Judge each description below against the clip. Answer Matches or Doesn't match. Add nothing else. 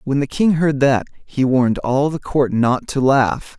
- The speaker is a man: Matches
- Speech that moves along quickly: Matches